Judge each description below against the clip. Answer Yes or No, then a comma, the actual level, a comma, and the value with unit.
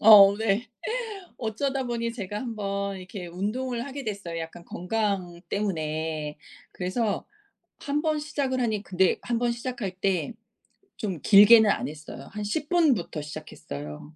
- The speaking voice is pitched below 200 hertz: No, high, 205 Hz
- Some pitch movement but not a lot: Yes, average, 5.0 semitones